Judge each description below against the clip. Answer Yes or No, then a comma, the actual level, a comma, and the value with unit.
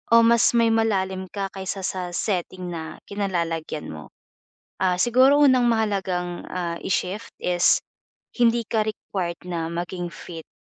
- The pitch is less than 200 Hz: Yes, high, 190 Hz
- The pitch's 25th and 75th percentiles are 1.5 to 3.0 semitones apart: No, average, 4.1 semitones